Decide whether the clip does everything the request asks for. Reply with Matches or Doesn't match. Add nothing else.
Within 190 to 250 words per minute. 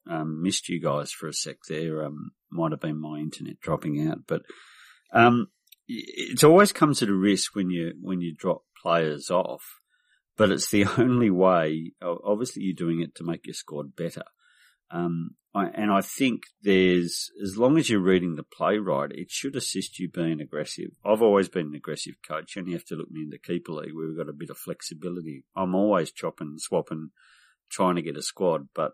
Matches